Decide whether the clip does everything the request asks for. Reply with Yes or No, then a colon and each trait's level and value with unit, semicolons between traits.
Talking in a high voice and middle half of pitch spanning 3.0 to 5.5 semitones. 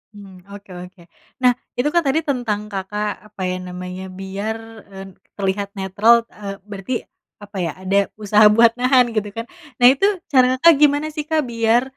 Yes: high, 210 Hz; average, 4.4 semitones